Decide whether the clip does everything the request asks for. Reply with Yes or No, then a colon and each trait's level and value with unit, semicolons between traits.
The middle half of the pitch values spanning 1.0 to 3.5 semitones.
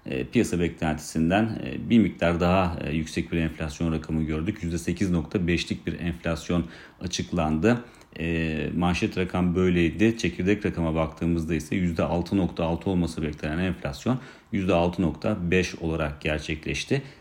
Yes: narrow, 2.4 semitones